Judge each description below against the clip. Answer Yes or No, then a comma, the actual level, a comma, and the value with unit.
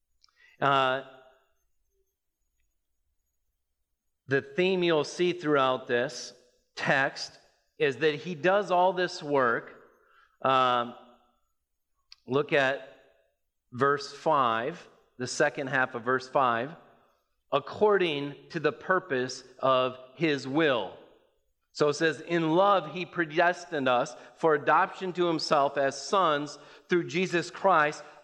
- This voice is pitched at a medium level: Yes, medium, 145 Hz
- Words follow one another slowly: Yes, slow, 105 wpm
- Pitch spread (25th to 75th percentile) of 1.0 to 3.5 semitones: No, average, 5.3 semitones